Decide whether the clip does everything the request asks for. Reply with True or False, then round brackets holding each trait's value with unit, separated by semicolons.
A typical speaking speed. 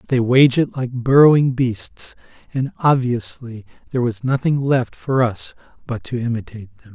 True (155 wpm)